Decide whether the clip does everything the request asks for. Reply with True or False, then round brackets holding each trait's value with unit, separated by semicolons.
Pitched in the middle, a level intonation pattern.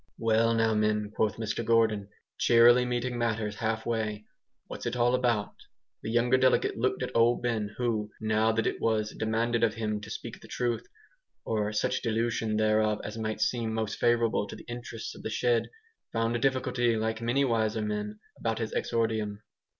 False (115 Hz; 1.7 semitones)